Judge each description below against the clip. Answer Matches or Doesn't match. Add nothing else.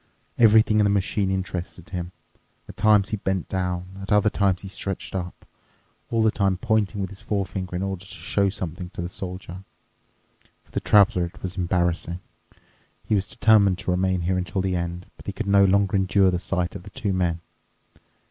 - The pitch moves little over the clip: Matches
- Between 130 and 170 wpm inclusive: Doesn't match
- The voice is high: Doesn't match